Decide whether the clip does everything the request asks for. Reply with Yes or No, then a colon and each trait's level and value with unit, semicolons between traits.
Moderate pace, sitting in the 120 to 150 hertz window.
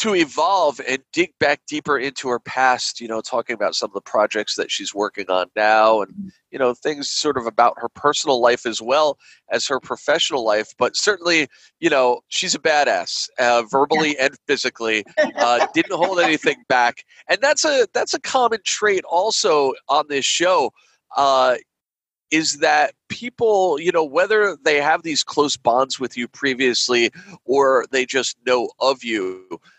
Yes: average, 175 wpm; low, 135 Hz